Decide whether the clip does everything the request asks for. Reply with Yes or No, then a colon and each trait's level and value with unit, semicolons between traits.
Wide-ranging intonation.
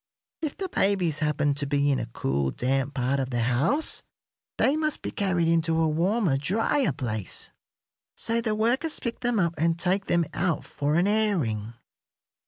Yes: wide, 7.6 semitones